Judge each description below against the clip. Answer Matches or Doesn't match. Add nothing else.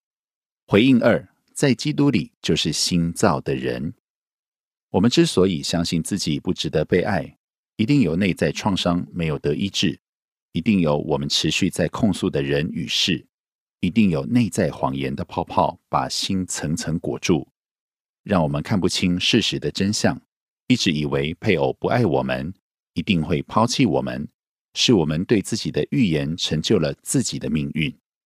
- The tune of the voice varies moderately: Doesn't match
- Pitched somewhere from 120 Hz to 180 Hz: Doesn't match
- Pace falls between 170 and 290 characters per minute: Matches